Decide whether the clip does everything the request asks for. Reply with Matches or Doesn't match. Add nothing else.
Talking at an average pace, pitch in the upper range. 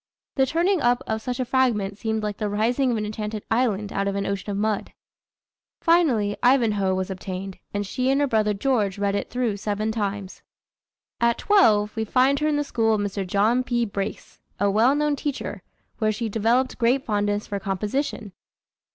Matches